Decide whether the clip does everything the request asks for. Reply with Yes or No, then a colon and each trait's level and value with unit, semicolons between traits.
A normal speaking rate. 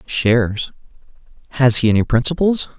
No: slow, 110 wpm